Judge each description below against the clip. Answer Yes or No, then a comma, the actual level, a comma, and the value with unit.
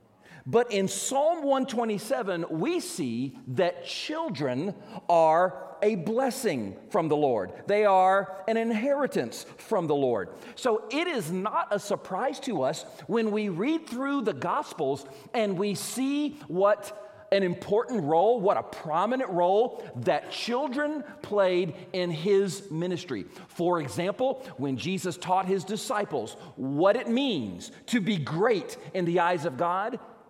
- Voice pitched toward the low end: No, high, 205 Hz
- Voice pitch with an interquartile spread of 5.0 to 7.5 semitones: Yes, wide, 5.4 semitones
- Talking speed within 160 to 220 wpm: No, average, 140 wpm